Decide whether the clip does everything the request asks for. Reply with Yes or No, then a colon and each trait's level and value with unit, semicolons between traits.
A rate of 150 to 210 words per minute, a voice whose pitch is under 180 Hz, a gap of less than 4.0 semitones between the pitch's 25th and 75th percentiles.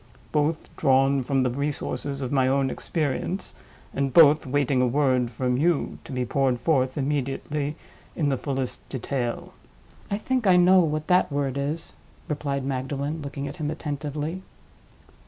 Yes: average, 155 wpm; medium, 140 Hz; narrow, 2.4 semitones